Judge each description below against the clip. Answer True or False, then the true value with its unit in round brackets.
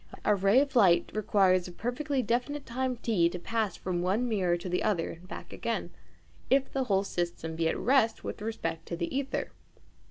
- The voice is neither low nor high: False (205 Hz)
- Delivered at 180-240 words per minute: True (195 wpm)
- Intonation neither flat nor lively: False (5.8 semitones)